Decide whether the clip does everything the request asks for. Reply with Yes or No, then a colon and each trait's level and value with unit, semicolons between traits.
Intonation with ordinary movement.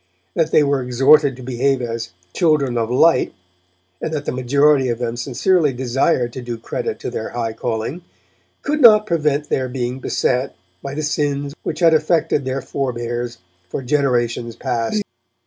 Yes: average, 3.8 semitones